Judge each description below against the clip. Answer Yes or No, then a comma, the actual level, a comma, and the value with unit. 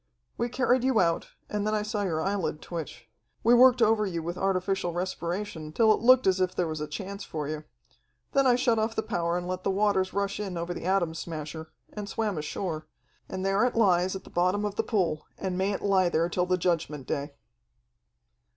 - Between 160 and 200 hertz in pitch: Yes, medium, 185 Hz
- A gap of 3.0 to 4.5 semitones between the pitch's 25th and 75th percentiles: Yes, average, 3.7 semitones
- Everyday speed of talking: No, fast, 215 wpm